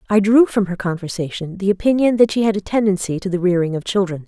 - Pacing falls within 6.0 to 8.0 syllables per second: Yes, 6.4 syllables/s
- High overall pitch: Yes, high, 195 Hz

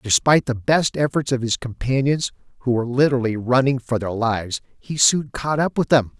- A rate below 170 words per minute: No, average, 195 wpm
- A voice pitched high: No, low, 125 Hz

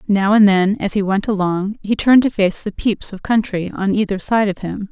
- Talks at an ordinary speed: No, fast, 245 wpm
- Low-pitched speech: No, high, 200 Hz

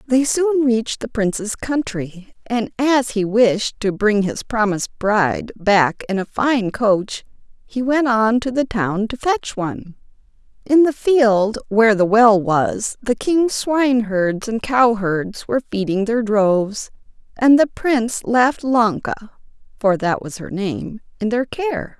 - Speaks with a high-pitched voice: Yes, high, 225 Hz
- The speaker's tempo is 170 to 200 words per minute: No, average, 160 wpm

